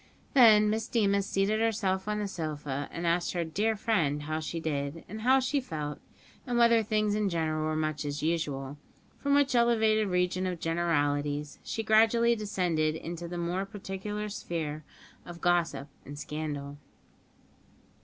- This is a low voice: No, medium, 175 Hz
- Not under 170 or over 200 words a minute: No, average, 155 wpm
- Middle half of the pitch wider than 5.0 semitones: Yes, wide, 5.5 semitones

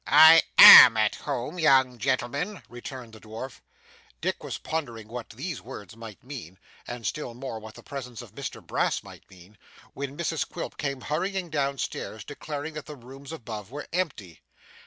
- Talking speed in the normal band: Yes, average, 170 wpm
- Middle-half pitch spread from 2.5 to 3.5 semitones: No, average, 4.7 semitones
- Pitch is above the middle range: No, low, 130 Hz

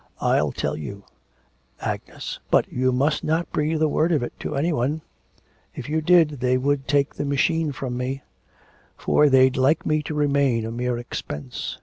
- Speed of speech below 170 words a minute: No, average, 180 wpm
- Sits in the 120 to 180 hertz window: Yes, medium, 140 Hz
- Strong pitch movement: No, average, 3.3 semitones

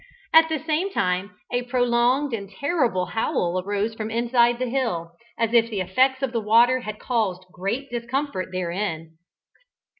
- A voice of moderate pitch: No, high, 230 Hz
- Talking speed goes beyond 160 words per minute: No, average, 155 wpm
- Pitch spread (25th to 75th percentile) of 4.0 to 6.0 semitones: Yes, average, 4.9 semitones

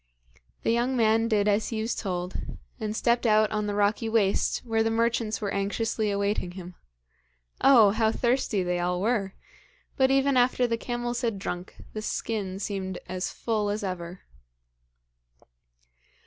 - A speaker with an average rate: Yes, average, 155 wpm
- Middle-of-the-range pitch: No, high, 215 Hz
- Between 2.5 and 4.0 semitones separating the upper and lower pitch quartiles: Yes, average, 2.9 semitones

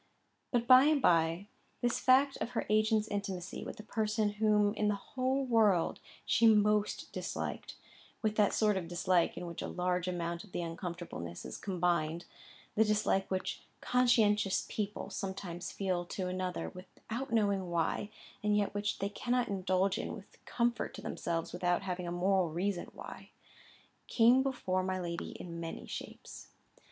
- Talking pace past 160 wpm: No, average, 155 wpm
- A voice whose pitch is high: Yes, high, 195 Hz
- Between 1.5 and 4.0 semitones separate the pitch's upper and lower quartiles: Yes, average, 3.4 semitones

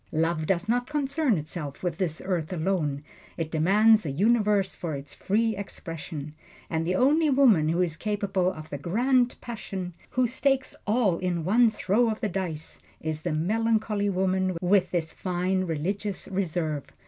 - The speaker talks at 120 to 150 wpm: No, average, 160 wpm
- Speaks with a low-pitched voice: No, medium, 185 Hz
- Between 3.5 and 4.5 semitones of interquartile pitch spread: No, average, 4.9 semitones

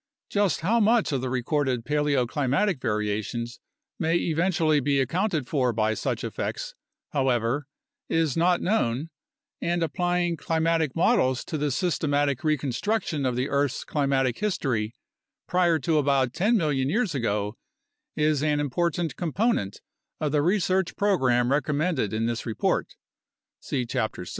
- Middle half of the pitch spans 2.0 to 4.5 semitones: No, average, 5.1 semitones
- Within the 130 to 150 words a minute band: Yes, average, 140 wpm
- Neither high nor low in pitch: Yes, medium, 145 Hz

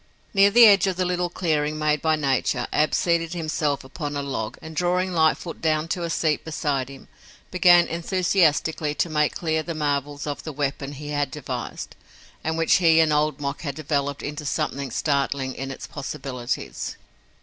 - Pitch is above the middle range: No, medium, 150 Hz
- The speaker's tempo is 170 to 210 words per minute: Yes, average, 180 wpm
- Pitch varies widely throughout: No, average, 2.8 semitones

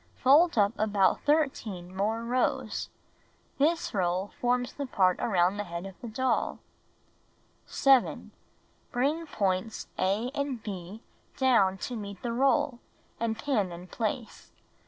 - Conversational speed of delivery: No, slow, 130 wpm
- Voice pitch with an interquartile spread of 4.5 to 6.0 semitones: Yes, average, 5.1 semitones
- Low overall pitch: No, high, 225 Hz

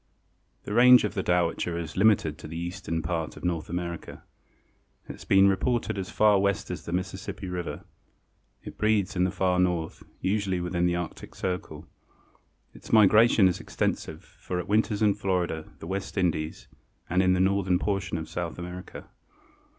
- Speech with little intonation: Yes, narrow, 2.3 semitones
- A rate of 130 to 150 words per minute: No, average, 175 wpm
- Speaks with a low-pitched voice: Yes, very low, 90 Hz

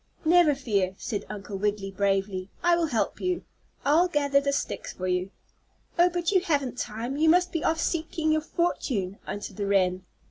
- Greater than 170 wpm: Yes, average, 180 wpm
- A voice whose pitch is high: Yes, very high, 275 Hz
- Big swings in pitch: Yes, wide, 8.7 semitones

